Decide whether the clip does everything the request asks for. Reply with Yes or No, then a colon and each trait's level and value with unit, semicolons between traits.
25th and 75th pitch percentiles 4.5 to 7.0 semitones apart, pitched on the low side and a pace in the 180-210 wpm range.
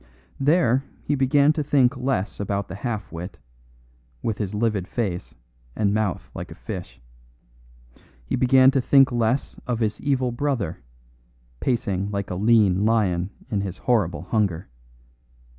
No: average, 4.8 semitones; low, 110 Hz; average, 140 wpm